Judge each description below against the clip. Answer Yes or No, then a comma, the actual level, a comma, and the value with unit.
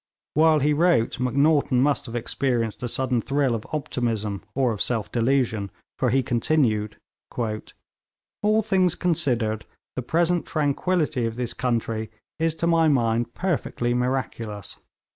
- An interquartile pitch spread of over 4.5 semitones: Yes, average, 5.0 semitones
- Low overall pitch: Yes, low, 125 Hz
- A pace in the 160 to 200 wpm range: No, slow, 135 wpm